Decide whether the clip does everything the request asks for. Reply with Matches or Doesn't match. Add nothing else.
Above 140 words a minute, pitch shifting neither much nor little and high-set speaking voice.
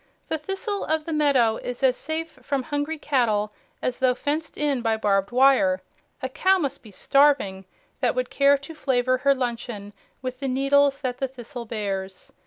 Matches